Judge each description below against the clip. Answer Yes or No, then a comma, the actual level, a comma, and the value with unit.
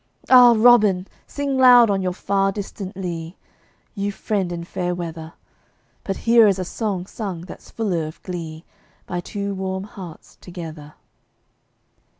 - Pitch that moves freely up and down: No, average, 3.2 semitones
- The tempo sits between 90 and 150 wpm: Yes, average, 145 wpm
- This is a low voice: No, high, 190 Hz